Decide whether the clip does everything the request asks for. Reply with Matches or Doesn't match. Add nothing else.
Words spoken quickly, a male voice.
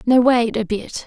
Doesn't match